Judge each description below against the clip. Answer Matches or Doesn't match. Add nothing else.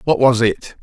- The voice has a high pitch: Doesn't match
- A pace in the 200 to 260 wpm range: Matches